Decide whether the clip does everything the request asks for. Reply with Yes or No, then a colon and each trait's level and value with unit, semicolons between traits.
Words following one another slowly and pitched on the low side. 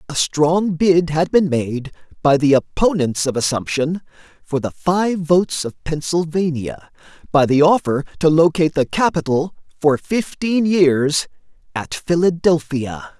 No: slow, 130 wpm; medium, 160 Hz